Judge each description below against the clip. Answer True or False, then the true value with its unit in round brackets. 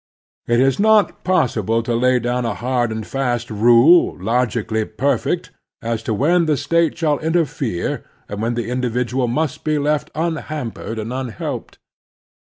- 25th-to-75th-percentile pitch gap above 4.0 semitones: True (4.5 semitones)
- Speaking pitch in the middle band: False (125 Hz)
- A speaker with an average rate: True (150 wpm)